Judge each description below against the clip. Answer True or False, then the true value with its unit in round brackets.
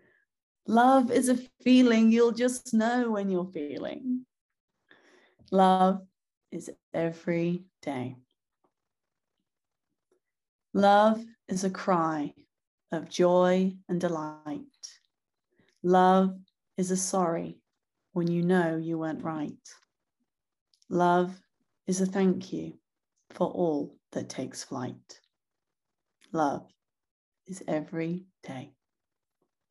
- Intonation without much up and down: False (4.7 semitones)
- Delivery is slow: True (95 wpm)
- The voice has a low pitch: False (185 Hz)